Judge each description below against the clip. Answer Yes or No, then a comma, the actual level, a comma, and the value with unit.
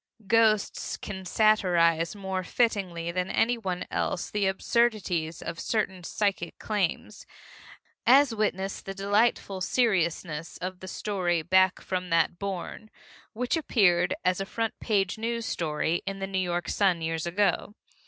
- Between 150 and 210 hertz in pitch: Yes, high, 190 Hz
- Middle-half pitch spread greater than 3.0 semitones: Yes, average, 3.5 semitones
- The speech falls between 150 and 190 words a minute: No, slow, 135 wpm